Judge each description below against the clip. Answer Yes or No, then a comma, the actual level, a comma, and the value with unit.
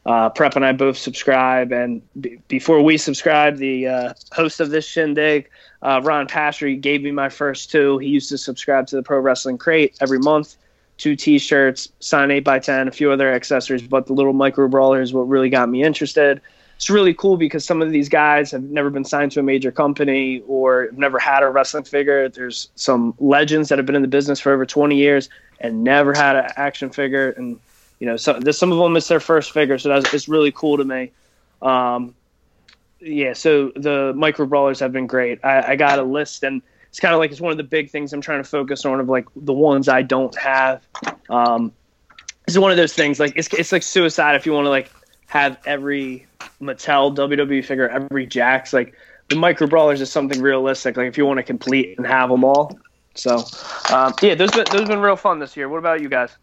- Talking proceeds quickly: Yes, fast, 225 wpm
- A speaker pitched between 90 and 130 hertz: No, medium, 140 Hz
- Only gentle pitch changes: Yes, narrow, 2.2 semitones